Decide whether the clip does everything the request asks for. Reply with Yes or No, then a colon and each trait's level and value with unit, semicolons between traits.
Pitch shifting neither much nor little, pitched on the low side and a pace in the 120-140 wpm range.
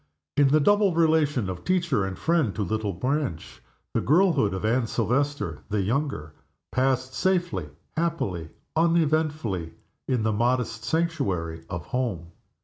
No: wide, 8.2 semitones; low, 125 Hz; slow, 135 wpm